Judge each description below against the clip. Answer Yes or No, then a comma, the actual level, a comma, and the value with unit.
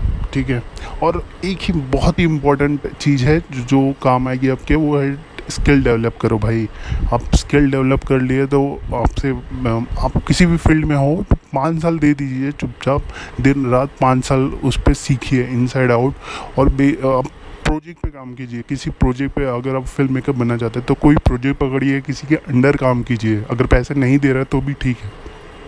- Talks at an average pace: No, fast, 195 wpm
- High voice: No, low, 135 Hz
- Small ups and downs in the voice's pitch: Yes, narrow, 2.2 semitones